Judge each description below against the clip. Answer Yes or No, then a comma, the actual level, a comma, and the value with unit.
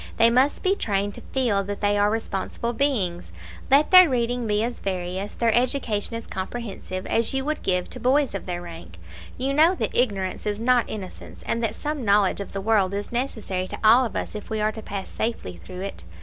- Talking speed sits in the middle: No, fast, 215 wpm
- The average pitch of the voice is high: Yes, high, 220 Hz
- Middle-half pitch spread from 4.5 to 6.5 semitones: No, average, 3.9 semitones